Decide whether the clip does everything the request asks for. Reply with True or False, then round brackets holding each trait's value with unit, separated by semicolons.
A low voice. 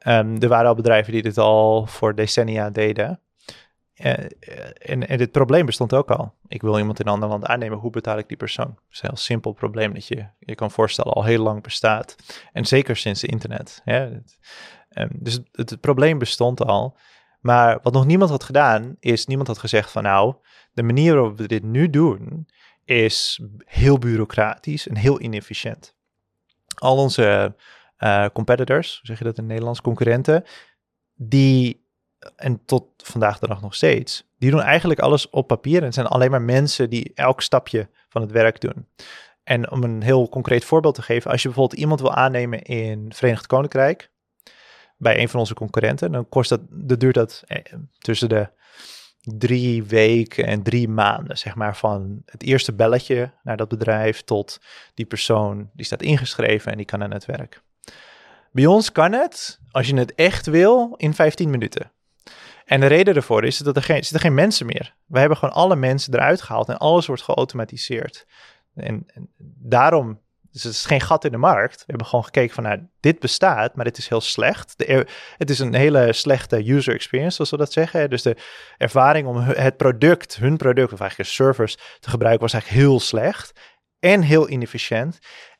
True (120 Hz)